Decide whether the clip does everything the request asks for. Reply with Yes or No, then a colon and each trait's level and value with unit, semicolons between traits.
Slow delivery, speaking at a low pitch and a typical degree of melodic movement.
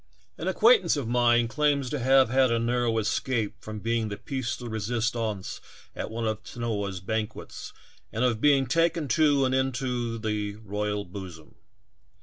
No: average, 155 wpm; low, 115 Hz; average, 3.5 semitones